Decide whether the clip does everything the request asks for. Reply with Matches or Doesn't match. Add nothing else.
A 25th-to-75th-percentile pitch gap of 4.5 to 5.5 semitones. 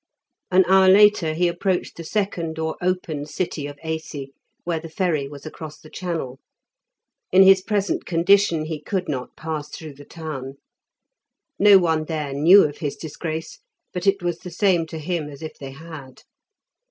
Doesn't match